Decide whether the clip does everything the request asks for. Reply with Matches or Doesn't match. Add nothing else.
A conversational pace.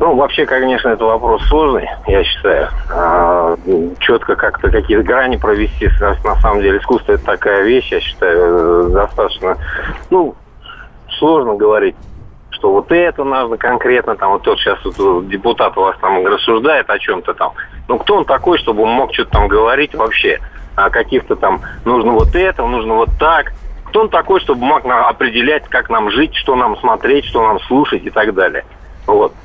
Doesn't match